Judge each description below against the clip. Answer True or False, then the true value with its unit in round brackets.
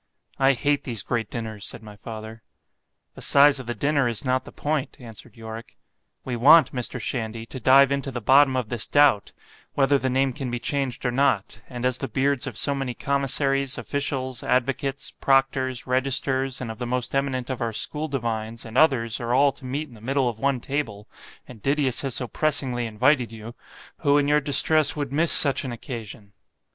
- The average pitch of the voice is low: True (130 Hz)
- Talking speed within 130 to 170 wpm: False (185 wpm)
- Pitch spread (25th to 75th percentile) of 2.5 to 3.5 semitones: True (2.9 semitones)